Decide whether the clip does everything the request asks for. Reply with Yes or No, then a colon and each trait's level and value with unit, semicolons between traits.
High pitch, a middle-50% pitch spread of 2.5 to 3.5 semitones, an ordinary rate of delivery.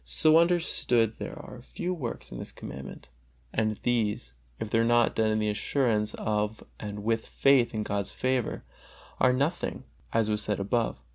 No: low, 115 Hz; average, 3.1 semitones; average, 170 wpm